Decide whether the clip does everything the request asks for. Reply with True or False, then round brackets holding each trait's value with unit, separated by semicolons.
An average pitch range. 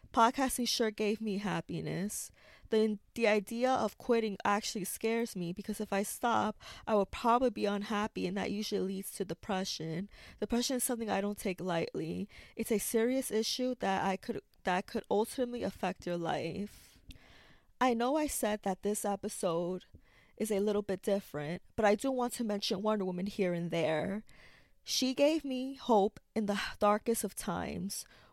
True (3.0 semitones)